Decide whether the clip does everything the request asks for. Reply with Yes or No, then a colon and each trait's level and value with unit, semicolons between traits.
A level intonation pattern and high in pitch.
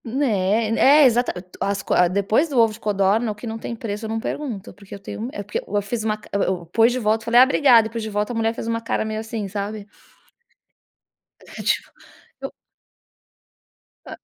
Yes: narrow, 2.3 semitones; high, 220 Hz